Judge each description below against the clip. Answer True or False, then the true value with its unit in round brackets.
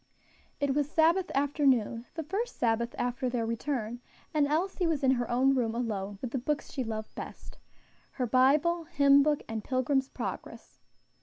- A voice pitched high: True (265 Hz)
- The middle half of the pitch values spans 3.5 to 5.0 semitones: True (3.8 semitones)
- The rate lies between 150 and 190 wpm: True (160 wpm)